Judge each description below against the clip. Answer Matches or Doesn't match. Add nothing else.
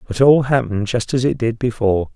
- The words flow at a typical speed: Doesn't match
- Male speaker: Matches